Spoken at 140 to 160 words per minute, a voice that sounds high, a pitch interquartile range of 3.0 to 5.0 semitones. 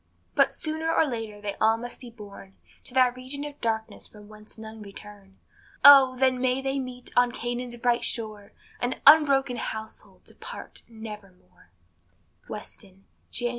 Yes: average, 155 wpm; high, 240 Hz; average, 3.4 semitones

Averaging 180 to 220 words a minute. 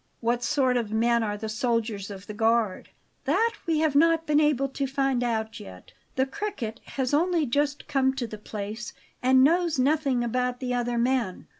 Yes: average, 185 wpm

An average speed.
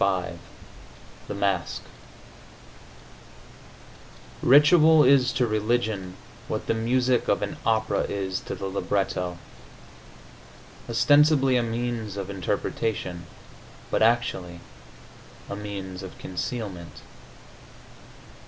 No: slow, 90 wpm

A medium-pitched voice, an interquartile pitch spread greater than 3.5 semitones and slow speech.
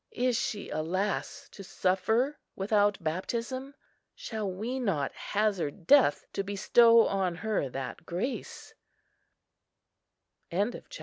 No: high, 205 Hz; average, 4.1 semitones; slow, 100 wpm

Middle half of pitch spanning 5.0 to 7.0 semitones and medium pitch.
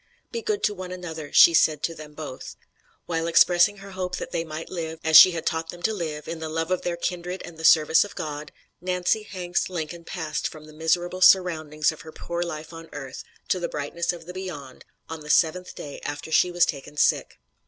No: narrow, 2.5 semitones; medium, 165 Hz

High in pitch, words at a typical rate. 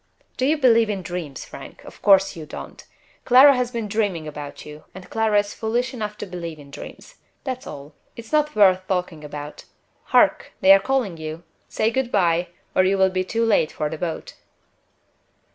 Yes: high, 195 Hz; average, 190 wpm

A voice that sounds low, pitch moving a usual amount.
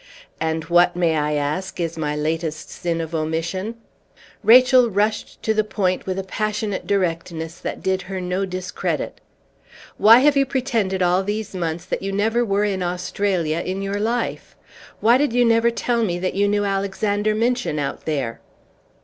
No: high, 190 Hz; average, 4.2 semitones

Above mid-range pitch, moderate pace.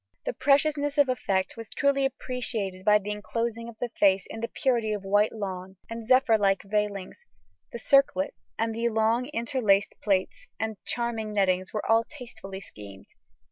Yes: high, 220 Hz; average, 165 wpm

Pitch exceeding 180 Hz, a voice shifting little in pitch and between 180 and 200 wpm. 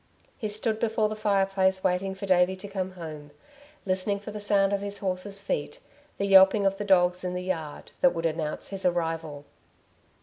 Yes: high, 190 Hz; narrow, 2.1 semitones; average, 190 wpm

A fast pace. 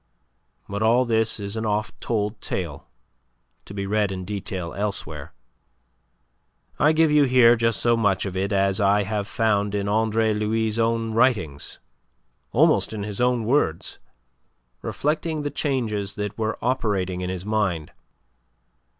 No: average, 145 wpm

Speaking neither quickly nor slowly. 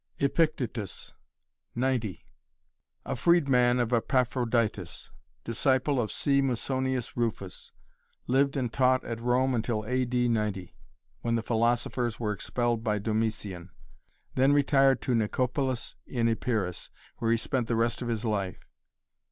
No: slow, 130 wpm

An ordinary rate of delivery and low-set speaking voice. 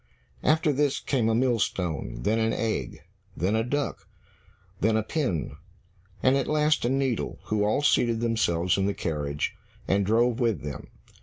Yes: average, 160 wpm; low, 115 Hz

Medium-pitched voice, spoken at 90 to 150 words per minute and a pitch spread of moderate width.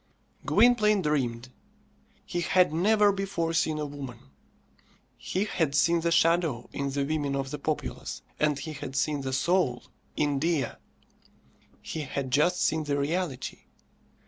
Yes: medium, 150 Hz; average, 140 wpm; average, 3.8 semitones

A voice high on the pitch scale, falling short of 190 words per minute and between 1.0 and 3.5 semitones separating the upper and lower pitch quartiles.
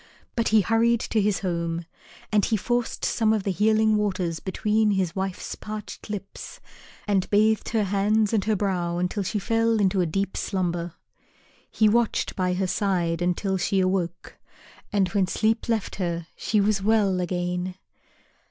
Yes: high, 195 Hz; average, 160 wpm; average, 2.9 semitones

